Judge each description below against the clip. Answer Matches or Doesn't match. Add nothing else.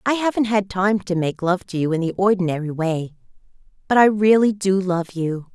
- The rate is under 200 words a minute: Doesn't match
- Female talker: Matches